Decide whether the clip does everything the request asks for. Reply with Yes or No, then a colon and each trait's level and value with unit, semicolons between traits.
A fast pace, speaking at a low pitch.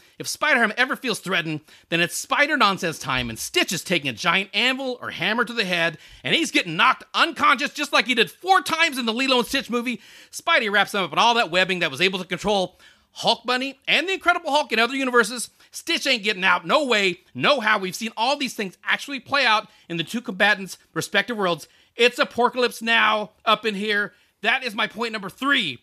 No: fast, 225 wpm; high, 225 Hz